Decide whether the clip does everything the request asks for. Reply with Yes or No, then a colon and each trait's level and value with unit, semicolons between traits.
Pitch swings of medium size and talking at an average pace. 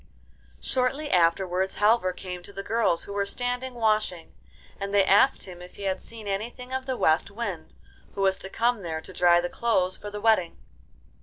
Yes: average, 4.2 semitones; average, 190 wpm